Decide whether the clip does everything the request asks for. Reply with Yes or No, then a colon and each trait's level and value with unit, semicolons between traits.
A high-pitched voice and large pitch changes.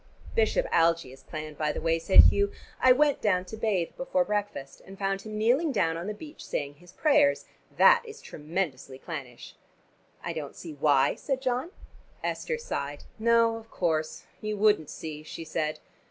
Yes: high, 195 Hz; wide, 7.1 semitones